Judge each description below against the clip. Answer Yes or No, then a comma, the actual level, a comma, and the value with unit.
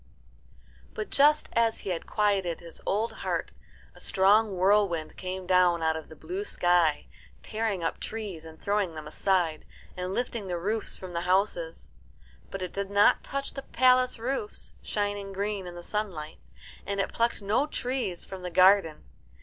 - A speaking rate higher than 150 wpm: Yes, average, 170 wpm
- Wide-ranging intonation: No, average, 3.8 semitones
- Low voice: No, high, 195 Hz